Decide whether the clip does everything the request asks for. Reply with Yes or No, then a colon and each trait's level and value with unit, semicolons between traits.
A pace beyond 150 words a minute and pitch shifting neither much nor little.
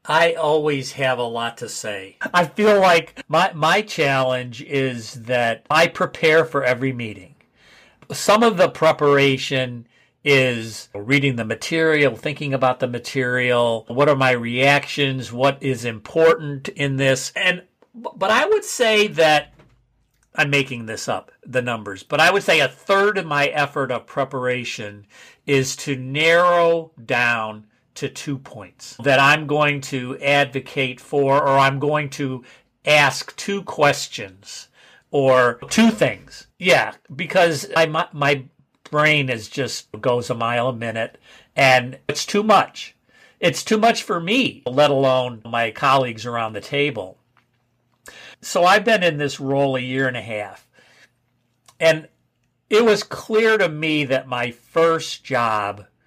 No: average, 145 wpm; average, 4.2 semitones